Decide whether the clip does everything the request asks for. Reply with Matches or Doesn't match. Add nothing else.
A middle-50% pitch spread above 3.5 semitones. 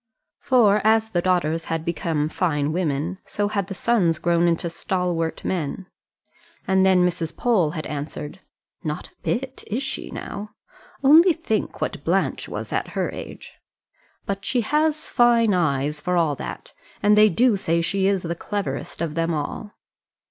Matches